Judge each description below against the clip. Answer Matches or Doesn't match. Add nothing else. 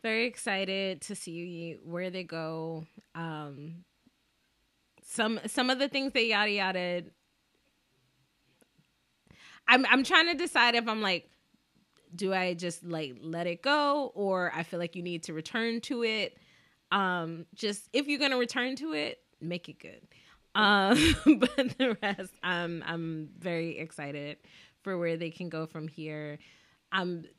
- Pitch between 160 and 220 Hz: Matches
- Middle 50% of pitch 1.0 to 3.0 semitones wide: Doesn't match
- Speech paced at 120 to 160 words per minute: Matches